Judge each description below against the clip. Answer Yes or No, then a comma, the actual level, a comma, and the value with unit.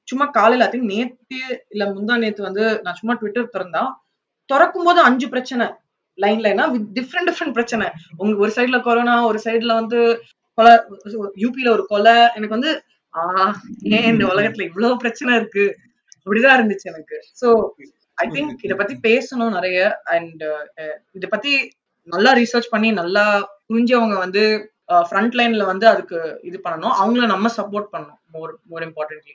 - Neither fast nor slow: No, fast, 145 wpm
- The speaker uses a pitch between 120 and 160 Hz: No, high, 225 Hz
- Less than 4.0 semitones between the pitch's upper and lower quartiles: Yes, average, 3.2 semitones